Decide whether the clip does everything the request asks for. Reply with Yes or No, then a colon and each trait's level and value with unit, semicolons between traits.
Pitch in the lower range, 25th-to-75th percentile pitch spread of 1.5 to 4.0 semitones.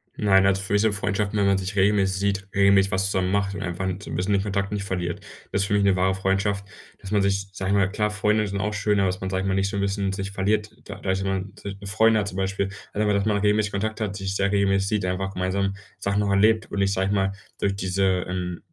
No: low, 100 Hz; narrow, 1.1 semitones